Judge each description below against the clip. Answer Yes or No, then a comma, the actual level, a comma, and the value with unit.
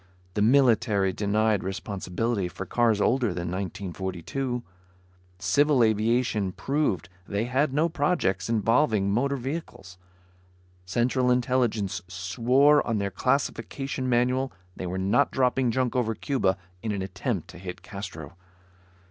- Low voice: Yes, low, 115 Hz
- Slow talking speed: Yes, slow, 120 wpm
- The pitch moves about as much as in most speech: Yes, average, 5.0 semitones